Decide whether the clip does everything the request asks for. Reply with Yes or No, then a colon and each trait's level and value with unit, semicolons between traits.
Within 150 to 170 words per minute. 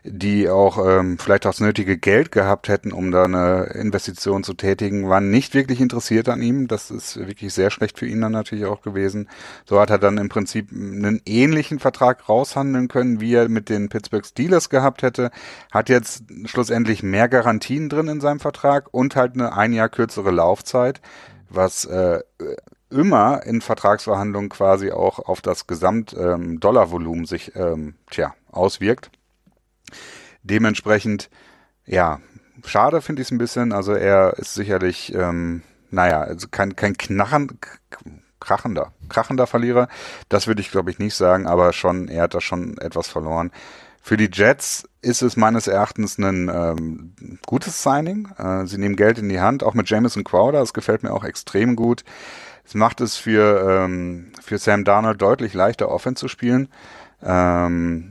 Yes: average, 165 wpm